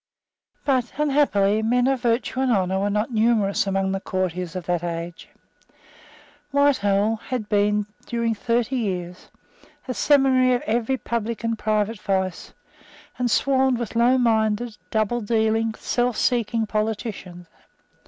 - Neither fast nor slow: No, slow, 125 wpm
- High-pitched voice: Yes, high, 220 Hz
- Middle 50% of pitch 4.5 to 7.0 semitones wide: No, average, 3.3 semitones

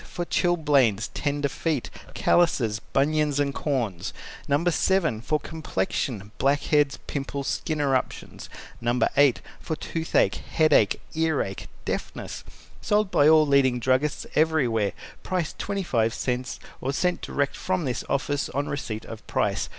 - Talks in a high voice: No, medium, 140 Hz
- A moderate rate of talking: No, slow, 125 wpm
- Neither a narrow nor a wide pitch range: Yes, average, 4.1 semitones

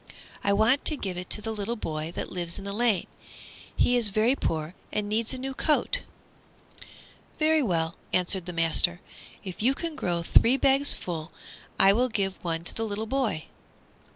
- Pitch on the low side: No, high, 205 Hz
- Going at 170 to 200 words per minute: Yes, average, 180 wpm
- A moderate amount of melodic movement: No, wide, 5.8 semitones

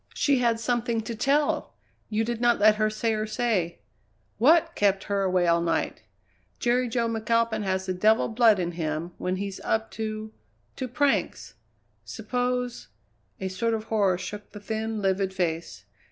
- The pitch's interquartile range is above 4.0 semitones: No, average, 3.7 semitones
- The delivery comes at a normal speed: Yes, average, 170 wpm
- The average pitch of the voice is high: Yes, high, 215 Hz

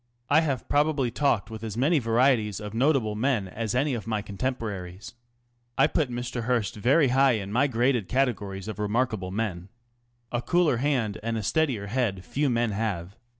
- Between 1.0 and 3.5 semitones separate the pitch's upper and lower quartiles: No, average, 4.1 semitones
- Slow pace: No, average, 175 wpm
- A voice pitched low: Yes, low, 115 Hz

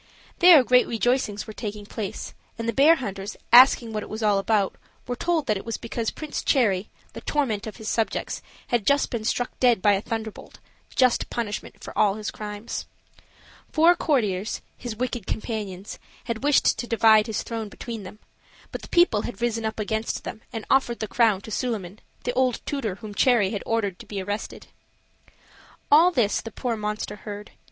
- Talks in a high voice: Yes, high, 225 Hz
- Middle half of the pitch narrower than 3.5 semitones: Yes, average, 2.9 semitones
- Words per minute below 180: No, average, 185 wpm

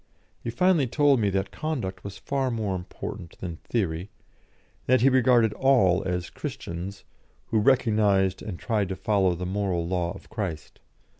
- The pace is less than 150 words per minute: No, average, 160 wpm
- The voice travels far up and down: No, average, 5.0 semitones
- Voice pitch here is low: Yes, low, 100 Hz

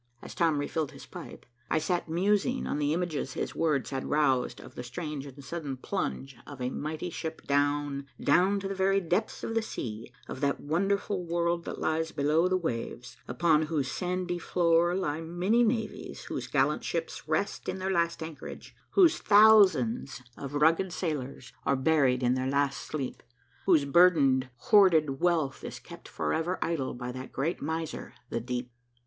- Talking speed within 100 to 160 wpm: No, average, 170 wpm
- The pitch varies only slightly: No, average, 4.5 semitones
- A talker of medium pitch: Yes, medium, 160 Hz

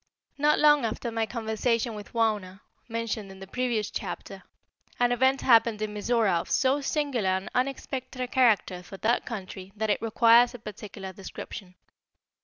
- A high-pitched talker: Yes, high, 225 Hz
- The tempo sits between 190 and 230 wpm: No, average, 160 wpm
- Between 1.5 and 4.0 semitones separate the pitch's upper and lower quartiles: Yes, average, 3.2 semitones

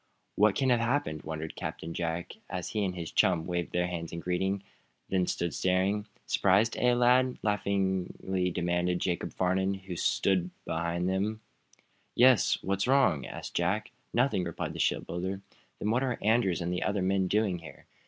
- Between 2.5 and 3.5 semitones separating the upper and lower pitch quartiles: Yes, average, 3.1 semitones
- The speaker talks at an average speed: Yes, average, 175 wpm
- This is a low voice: Yes, very low, 95 Hz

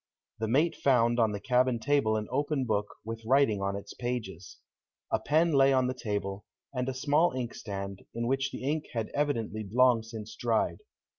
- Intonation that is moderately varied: Yes, average, 3.8 semitones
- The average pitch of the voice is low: Yes, low, 120 Hz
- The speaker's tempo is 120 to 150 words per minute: No, average, 180 wpm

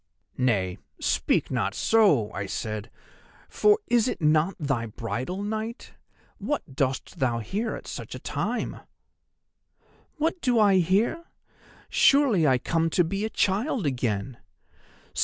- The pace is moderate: No, slow, 130 wpm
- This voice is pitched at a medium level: Yes, medium, 170 Hz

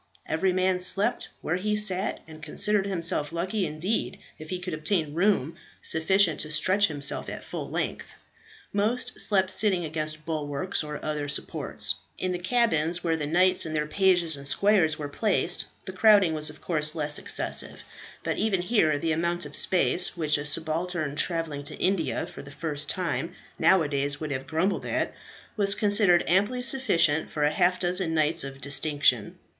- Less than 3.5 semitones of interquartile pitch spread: No, average, 3.8 semitones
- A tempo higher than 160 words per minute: Yes, average, 170 wpm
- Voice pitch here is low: No, medium, 170 Hz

